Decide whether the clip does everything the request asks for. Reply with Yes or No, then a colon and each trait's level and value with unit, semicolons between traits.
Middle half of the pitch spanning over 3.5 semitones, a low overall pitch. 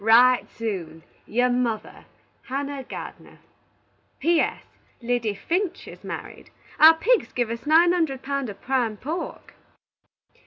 No: wide, 5.4 semitones; very high, 255 Hz